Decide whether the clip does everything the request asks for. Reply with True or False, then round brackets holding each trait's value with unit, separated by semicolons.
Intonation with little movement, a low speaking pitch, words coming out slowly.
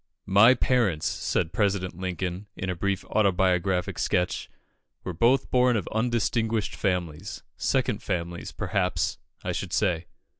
False (3.8 semitones; 95 Hz; 125 wpm)